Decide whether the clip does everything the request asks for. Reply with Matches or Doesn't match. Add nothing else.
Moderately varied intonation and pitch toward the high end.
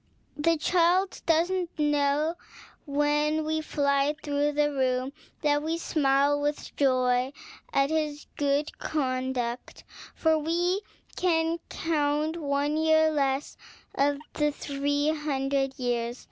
Doesn't match